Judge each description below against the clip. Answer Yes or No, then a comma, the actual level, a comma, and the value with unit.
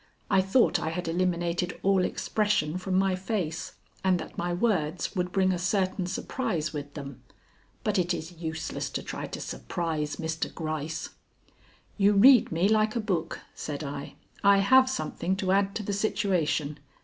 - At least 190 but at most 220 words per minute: No, average, 165 wpm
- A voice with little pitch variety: No, average, 3.5 semitones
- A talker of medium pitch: Yes, medium, 180 Hz